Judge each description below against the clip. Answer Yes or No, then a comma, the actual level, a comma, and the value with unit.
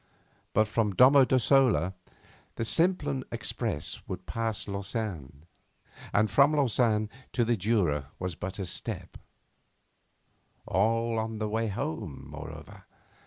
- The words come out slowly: Yes, slow, 120 wpm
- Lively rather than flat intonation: No, average, 3.7 semitones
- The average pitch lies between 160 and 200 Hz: No, low, 110 Hz